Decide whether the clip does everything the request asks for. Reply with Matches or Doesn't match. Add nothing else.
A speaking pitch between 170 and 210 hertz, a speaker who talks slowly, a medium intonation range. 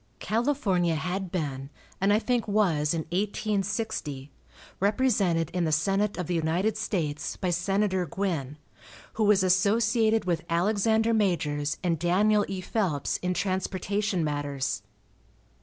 Matches